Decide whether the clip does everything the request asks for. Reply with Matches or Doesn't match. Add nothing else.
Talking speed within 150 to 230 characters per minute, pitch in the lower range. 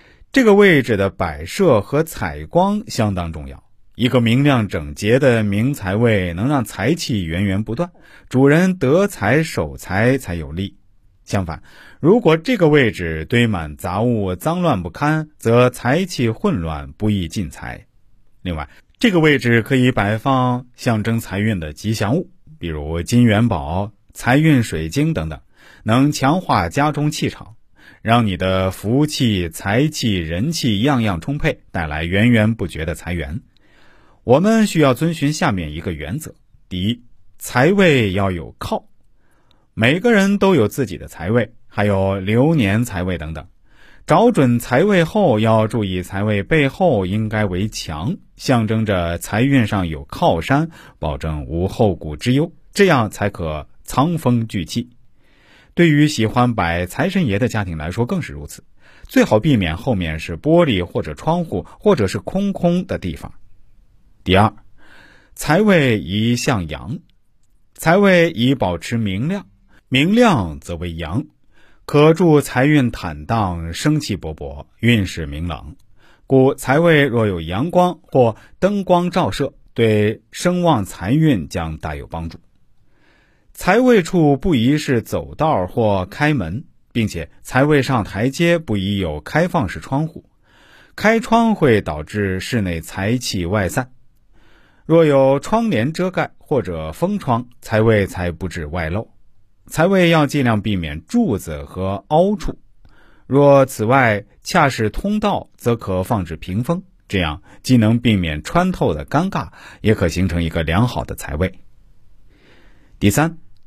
Matches